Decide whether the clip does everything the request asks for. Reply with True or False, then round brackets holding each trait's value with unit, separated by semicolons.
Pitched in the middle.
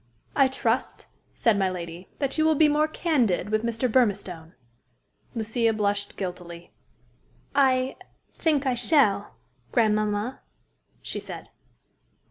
False (225 Hz)